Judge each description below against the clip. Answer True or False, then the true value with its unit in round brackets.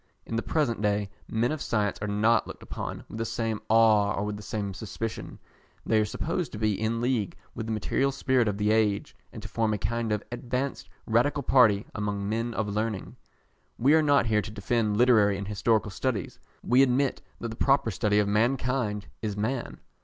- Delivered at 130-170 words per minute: False (200 wpm)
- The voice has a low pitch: True (110 Hz)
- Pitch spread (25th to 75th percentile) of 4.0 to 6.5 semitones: False (2.7 semitones)